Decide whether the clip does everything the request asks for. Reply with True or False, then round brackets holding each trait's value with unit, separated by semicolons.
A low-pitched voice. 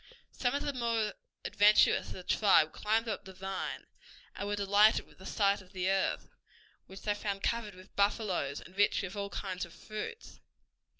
False (200 Hz)